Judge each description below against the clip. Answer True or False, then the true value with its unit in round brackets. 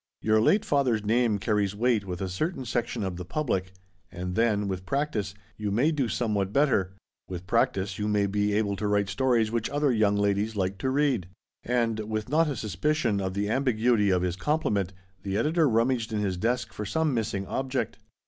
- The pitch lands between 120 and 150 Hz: False (110 Hz)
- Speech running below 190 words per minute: False (195 wpm)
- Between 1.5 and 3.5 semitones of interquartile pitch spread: False (4.0 semitones)